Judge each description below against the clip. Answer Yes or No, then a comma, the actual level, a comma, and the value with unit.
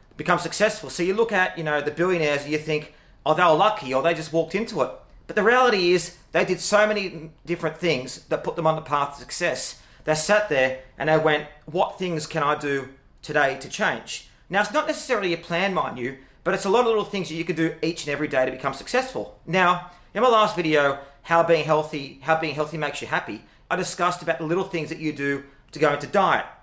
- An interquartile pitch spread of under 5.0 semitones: Yes, average, 3.8 semitones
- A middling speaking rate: No, fast, 245 wpm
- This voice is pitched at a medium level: Yes, medium, 160 Hz